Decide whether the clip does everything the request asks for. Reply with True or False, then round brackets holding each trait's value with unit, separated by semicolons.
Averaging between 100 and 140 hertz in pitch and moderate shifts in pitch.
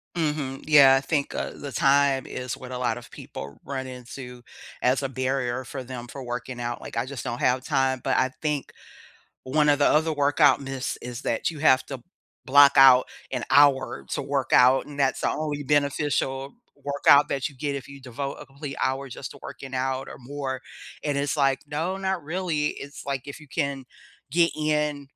False (135 Hz; 1.9 semitones)